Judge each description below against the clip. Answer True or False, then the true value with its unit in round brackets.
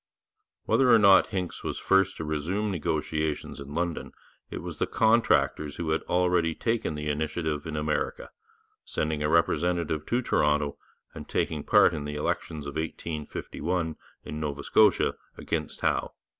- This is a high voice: False (80 Hz)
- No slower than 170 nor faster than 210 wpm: False (150 wpm)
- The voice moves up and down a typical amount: True (3.0 semitones)